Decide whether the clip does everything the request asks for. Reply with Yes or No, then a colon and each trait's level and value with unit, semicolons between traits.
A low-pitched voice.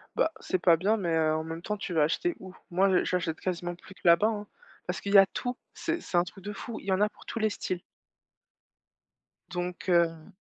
No: medium, 185 Hz